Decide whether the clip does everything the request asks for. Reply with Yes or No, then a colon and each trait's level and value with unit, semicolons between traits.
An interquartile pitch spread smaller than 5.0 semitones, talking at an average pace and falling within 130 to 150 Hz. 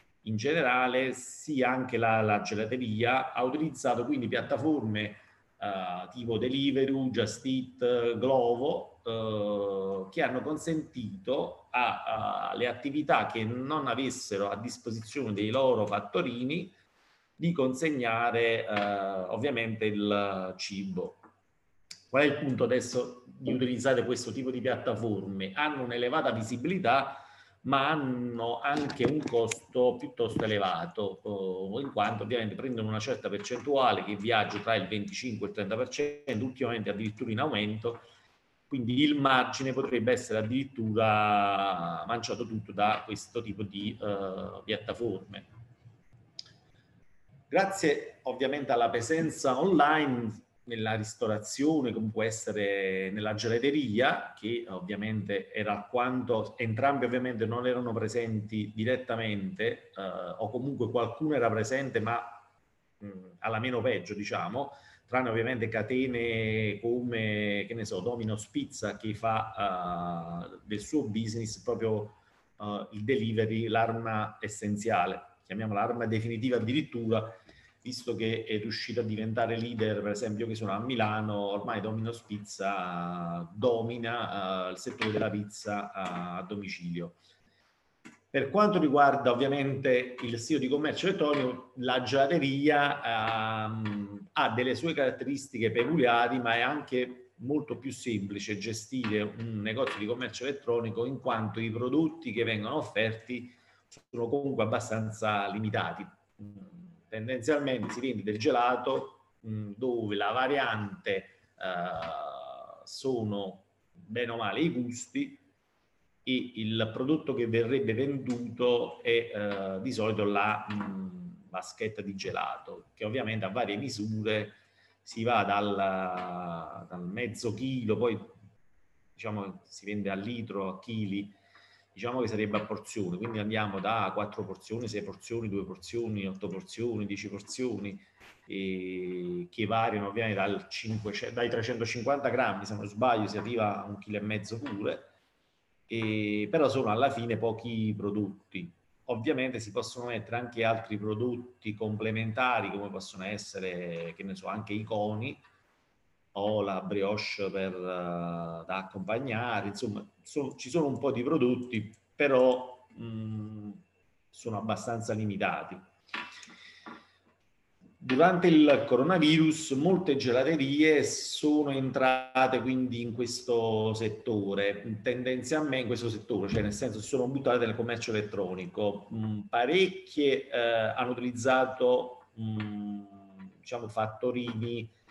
No: average, 3.5 semitones; average, 125 wpm; low, 115 Hz